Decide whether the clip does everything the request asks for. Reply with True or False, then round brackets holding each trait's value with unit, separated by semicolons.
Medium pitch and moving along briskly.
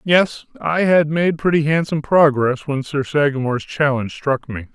False (150 Hz; 165 wpm)